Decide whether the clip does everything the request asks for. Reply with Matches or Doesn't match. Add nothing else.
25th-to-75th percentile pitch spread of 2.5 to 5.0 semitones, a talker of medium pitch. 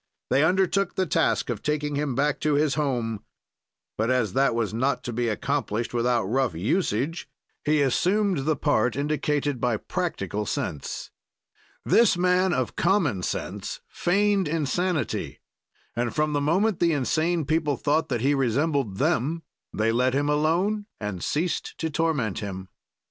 Doesn't match